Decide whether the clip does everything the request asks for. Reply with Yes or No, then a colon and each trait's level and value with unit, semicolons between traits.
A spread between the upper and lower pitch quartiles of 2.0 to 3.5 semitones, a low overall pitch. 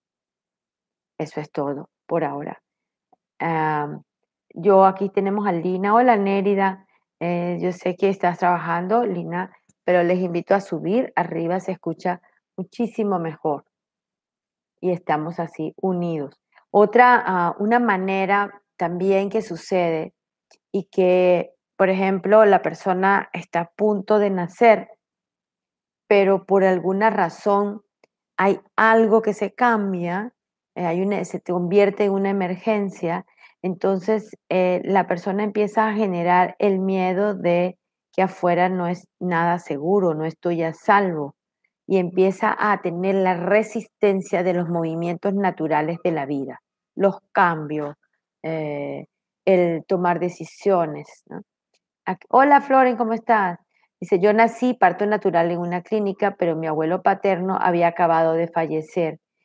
No: average, 2.8 semitones; medium, 185 Hz